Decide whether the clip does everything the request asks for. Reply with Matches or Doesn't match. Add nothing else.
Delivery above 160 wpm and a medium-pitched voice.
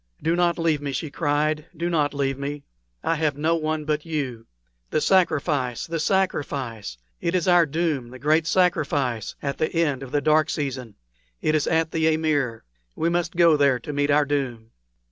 Matches